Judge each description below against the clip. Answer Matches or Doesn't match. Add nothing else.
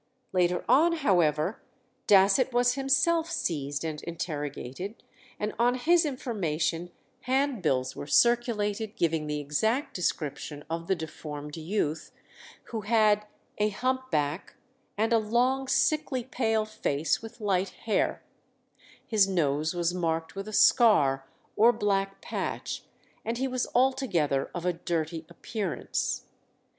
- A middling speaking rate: Doesn't match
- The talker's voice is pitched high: Matches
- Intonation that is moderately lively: Doesn't match